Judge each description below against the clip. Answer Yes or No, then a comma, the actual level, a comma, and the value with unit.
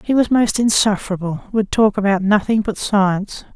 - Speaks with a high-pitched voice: Yes, high, 205 Hz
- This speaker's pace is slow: No, average, 170 wpm